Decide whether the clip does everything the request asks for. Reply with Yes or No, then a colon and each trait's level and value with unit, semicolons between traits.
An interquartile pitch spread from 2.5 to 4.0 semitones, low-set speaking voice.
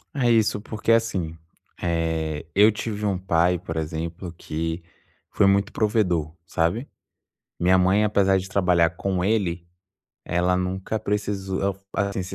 Yes: average, 3.3 semitones; very low, 95 Hz